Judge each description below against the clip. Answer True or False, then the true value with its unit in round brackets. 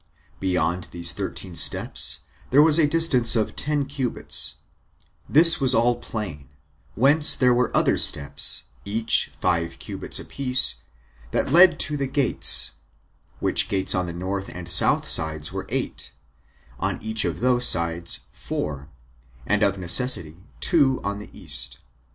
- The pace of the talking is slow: False (145 wpm)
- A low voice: True (110 Hz)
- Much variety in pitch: True (7.5 semitones)